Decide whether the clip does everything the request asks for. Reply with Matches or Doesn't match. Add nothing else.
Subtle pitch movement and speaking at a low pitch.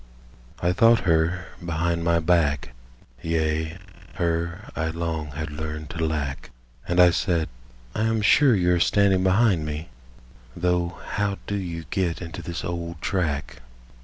Matches